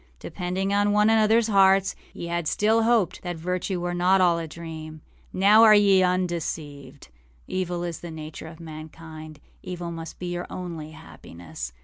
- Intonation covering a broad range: No, average, 3.3 semitones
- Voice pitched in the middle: Yes, medium, 175 Hz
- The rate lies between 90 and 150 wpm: No, average, 160 wpm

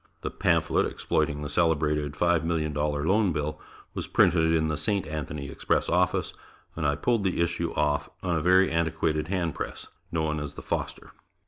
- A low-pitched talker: Yes, very low, 80 Hz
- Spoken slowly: No, average, 180 wpm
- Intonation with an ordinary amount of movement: No, narrow, 2.2 semitones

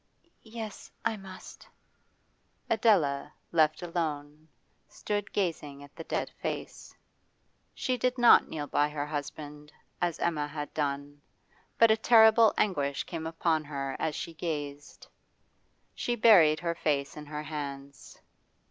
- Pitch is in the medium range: Yes, medium, 155 Hz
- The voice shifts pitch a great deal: No, average, 4.5 semitones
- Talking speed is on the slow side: Yes, slow, 130 wpm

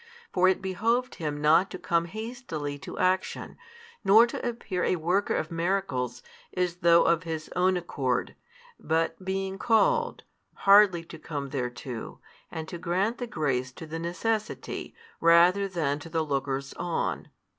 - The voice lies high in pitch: No, medium, 170 Hz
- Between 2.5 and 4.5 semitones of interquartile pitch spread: Yes, average, 3.9 semitones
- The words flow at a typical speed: Yes, average, 150 wpm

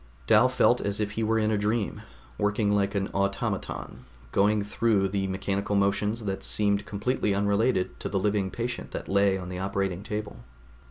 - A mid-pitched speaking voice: No, low, 100 Hz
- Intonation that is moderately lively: No, narrow, 1.5 semitones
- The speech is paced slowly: No, average, 170 wpm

